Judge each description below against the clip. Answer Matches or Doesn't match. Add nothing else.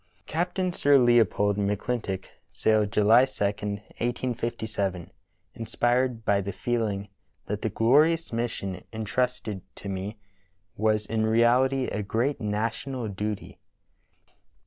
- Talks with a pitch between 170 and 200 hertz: Doesn't match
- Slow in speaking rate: Matches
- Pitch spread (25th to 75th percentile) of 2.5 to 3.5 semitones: Matches